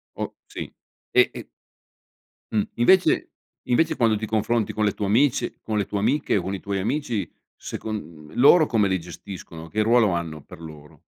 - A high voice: No, low, 105 Hz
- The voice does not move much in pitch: No, average, 4.6 semitones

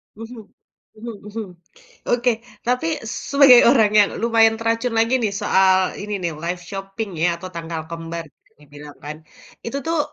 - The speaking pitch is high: Yes, high, 215 Hz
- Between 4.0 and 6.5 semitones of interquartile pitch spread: Yes, average, 5.2 semitones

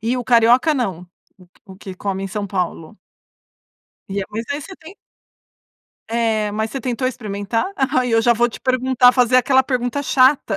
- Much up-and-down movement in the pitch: No, average, 3.7 semitones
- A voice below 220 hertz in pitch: No, high, 235 Hz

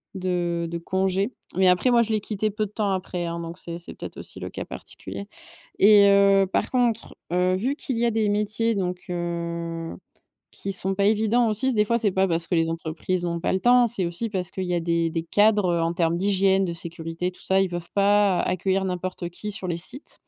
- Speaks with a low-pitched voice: No, high, 190 Hz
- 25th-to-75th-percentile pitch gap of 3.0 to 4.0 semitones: Yes, average, 3.3 semitones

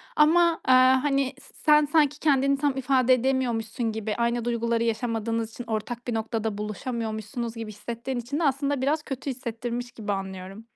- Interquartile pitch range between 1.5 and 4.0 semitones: Yes, average, 3.2 semitones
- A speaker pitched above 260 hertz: No, high, 240 Hz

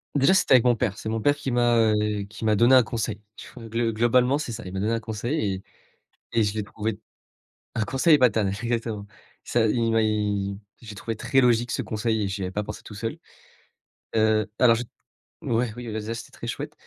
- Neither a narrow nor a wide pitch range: No, narrow, 2.1 semitones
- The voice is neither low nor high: No, low, 115 Hz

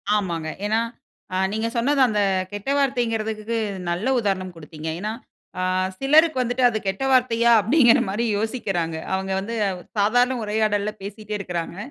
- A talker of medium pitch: No, high, 215 Hz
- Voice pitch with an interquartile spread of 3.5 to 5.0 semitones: Yes, average, 3.8 semitones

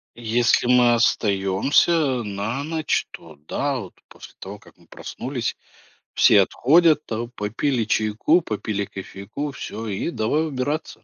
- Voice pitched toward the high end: No, low, 120 Hz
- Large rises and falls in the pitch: Yes, wide, 5.8 semitones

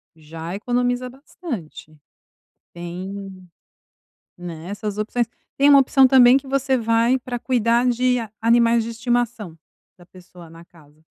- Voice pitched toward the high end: Yes, high, 230 Hz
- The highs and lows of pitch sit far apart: Yes, wide, 5.8 semitones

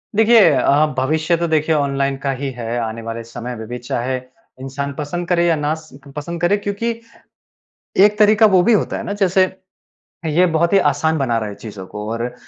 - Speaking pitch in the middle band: Yes, medium, 150 Hz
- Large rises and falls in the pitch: Yes, wide, 6.3 semitones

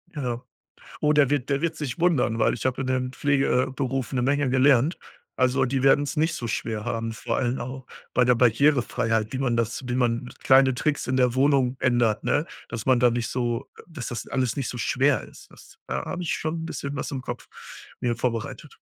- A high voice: No, low, 130 Hz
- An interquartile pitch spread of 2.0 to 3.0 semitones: Yes, narrow, 2.6 semitones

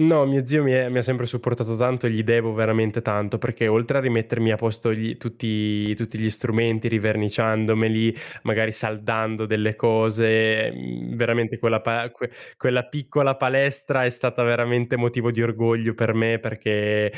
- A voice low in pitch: Yes, low, 115 Hz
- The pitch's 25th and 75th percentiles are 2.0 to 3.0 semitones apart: No, narrow, 1.6 semitones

